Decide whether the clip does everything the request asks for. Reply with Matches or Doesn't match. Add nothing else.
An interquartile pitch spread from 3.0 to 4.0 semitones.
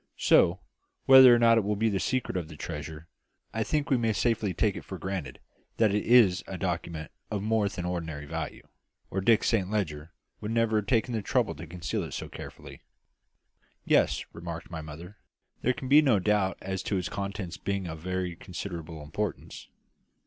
Doesn't match